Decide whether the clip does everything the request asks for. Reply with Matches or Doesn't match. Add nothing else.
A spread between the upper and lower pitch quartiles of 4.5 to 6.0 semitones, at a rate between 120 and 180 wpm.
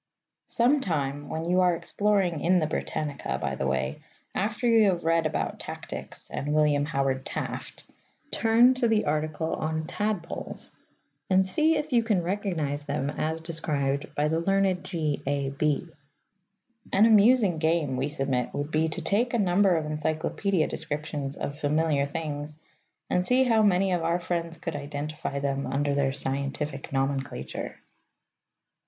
Matches